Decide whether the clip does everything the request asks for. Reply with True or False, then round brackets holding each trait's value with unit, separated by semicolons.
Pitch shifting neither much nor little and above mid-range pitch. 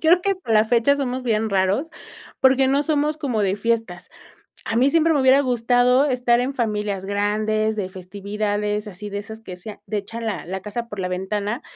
True (4.0 semitones; 220 Hz)